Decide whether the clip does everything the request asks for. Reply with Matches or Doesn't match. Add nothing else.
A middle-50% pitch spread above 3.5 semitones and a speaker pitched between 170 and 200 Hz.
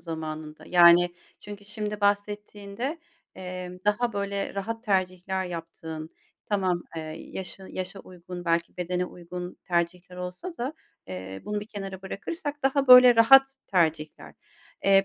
Doesn't match